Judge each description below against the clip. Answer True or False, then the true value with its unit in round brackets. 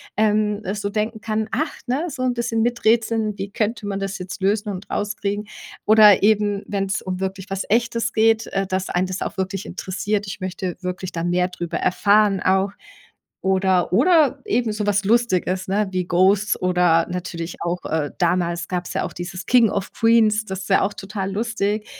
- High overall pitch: True (200 Hz)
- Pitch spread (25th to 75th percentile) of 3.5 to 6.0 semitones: False (2.7 semitones)